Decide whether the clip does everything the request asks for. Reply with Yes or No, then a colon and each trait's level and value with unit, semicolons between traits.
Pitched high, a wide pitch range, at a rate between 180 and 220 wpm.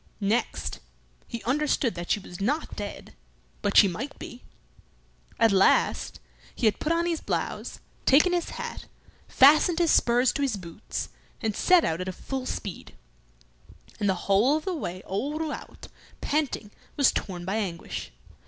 No: high, 240 Hz; wide, 7.4 semitones; average, 155 wpm